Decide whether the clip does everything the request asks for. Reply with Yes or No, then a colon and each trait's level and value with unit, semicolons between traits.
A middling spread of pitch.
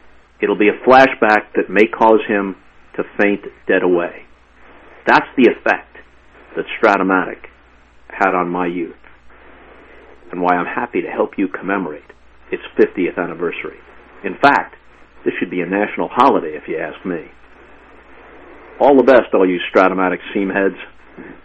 No: wide, 6.7 semitones